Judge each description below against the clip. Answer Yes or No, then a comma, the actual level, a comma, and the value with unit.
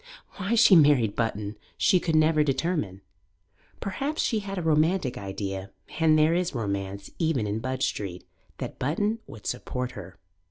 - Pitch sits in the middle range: Yes, medium, 145 Hz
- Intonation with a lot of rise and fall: Yes, wide, 8.9 semitones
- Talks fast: No, average, 155 wpm